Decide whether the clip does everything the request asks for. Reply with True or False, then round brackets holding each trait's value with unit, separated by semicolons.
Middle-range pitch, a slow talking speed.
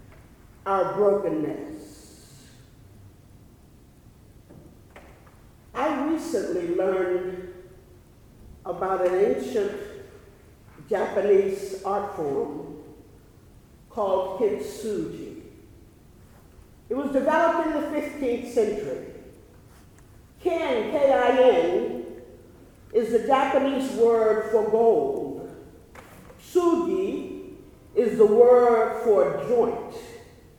False (230 Hz; 65 wpm)